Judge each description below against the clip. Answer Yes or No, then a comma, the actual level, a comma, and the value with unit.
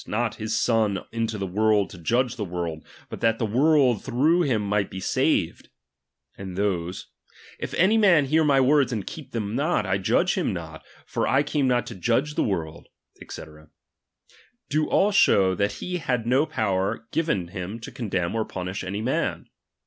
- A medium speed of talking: Yes, average, 180 wpm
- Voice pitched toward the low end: Yes, low, 115 Hz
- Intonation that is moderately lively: No, wide, 6.0 semitones